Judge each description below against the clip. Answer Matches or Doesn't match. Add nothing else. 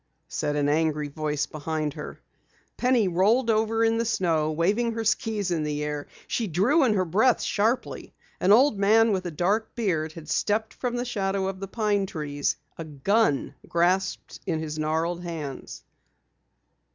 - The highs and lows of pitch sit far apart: Matches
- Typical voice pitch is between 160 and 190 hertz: Matches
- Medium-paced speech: Matches